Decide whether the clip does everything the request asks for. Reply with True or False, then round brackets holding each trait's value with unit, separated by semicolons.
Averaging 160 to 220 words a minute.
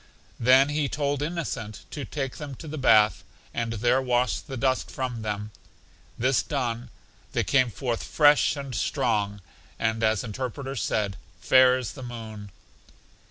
False (150 wpm)